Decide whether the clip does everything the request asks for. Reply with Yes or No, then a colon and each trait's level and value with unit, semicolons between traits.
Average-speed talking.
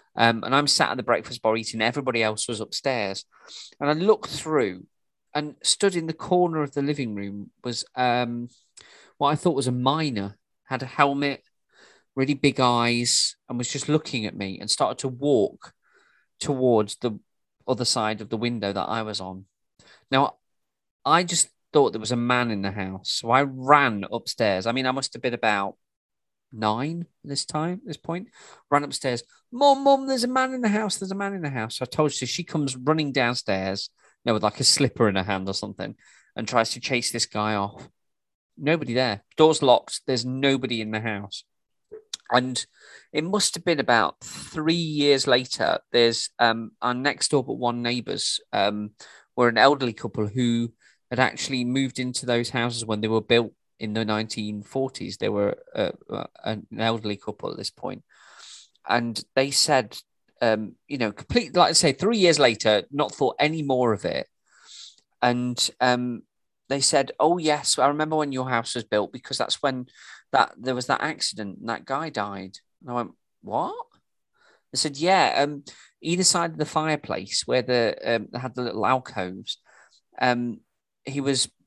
Yes: average, 185 wpm